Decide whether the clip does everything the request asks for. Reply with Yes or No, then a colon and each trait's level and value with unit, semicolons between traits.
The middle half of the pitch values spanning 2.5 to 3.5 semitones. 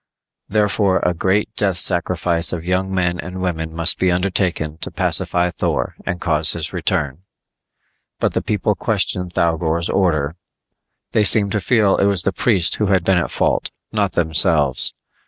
Yes: average, 2.9 semitones